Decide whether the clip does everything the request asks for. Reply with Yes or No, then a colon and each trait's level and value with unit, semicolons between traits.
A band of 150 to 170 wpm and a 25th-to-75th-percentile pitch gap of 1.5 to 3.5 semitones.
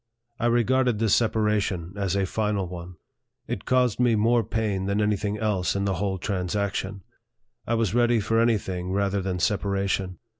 No: average, 185 wpm; average, 2.8 semitones